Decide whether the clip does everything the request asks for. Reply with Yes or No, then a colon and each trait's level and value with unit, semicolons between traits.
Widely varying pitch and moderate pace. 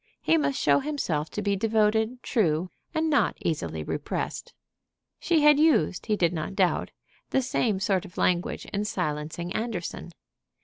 Yes: wide, 6.5 semitones; average, 150 wpm